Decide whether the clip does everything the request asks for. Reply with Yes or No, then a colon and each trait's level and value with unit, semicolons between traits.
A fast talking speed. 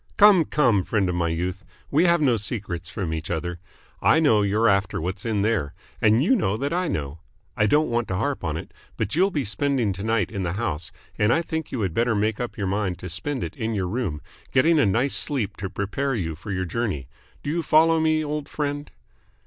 Yes: fast, 230 wpm